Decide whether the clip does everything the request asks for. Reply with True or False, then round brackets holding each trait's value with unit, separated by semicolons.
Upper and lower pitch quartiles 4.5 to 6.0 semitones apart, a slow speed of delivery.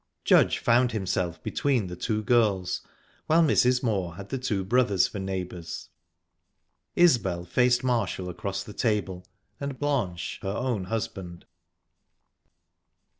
True (5.1 semitones; 125 wpm)